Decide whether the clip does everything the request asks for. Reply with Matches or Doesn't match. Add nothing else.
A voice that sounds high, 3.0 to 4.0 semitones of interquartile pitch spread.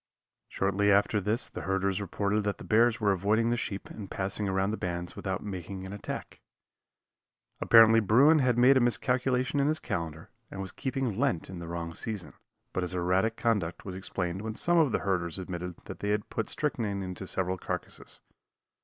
Doesn't match